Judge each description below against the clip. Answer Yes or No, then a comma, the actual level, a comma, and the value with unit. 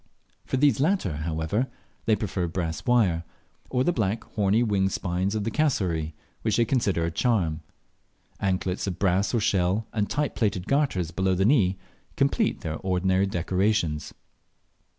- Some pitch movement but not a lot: Yes, average, 4.2 semitones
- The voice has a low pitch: Yes, very low, 95 Hz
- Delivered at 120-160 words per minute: Yes, average, 150 wpm